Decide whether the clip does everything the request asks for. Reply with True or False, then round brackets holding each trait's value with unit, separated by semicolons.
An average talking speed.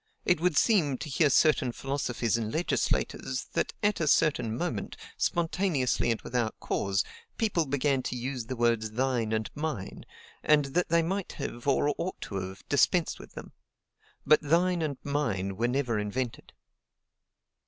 True (155 wpm)